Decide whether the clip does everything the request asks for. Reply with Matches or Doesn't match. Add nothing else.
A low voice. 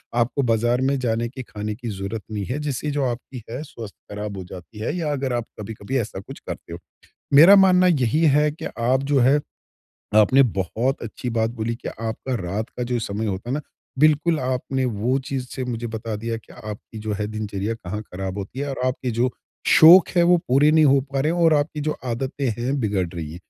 Matches